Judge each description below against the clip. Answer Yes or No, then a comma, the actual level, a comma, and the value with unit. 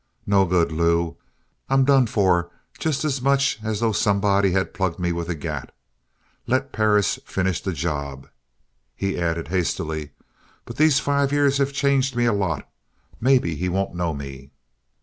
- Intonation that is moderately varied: No, wide, 7.5 semitones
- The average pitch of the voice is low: Yes, very low, 95 Hz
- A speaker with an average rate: Yes, average, 160 wpm